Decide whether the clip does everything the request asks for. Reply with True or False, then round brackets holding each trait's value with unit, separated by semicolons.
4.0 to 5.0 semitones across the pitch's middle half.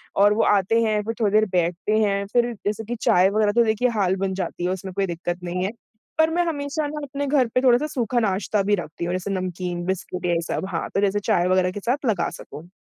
True (4.3 semitones)